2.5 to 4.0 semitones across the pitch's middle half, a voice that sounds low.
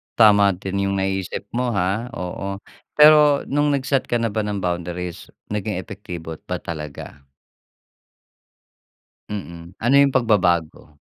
No: average, 5.0 semitones; low, 100 Hz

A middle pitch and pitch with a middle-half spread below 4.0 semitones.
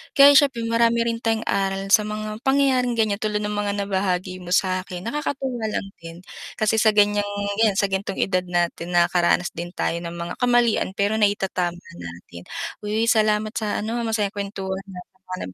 No: high, 205 Hz; average, 3.4 semitones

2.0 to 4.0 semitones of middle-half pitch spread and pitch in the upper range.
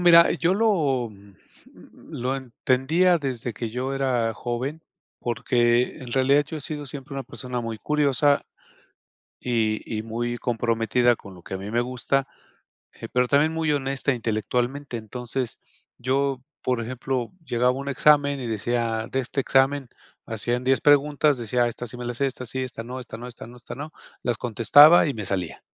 No: average, 2.9 semitones; low, 125 Hz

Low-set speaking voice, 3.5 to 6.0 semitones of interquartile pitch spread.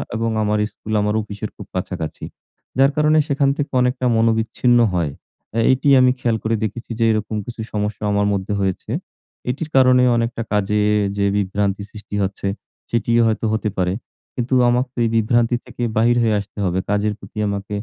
No: low, 110 Hz; average, 2.9 semitones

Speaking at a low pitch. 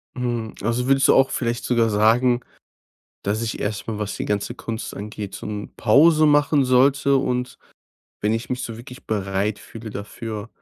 Yes: low, 115 Hz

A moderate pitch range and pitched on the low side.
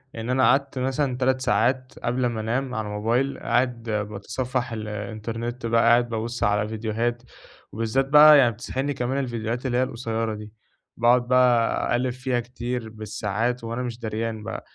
No: narrow, 2.3 semitones; low, 120 Hz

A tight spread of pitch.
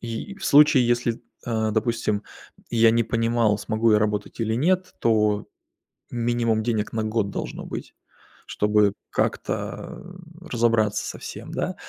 Yes: narrow, 1.8 semitones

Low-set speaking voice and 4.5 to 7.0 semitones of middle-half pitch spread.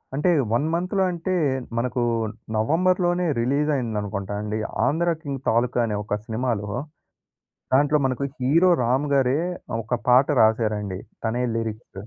Yes: low, 125 Hz; wide, 5.5 semitones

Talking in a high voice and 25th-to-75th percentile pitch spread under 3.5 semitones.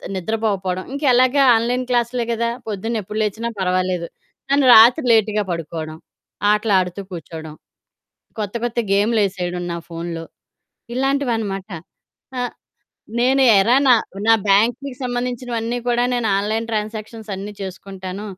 No: high, 215 Hz; average, 4.2 semitones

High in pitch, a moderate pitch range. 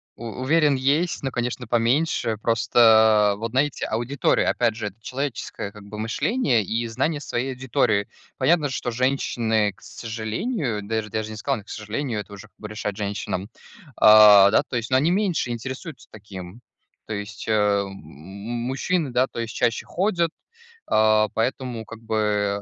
No: low, 115 Hz; average, 3.7 semitones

